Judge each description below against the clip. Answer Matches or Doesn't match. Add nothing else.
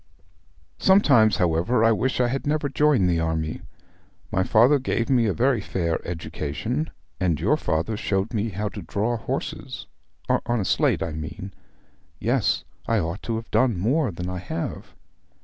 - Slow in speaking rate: Doesn't match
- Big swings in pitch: Matches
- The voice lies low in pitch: Matches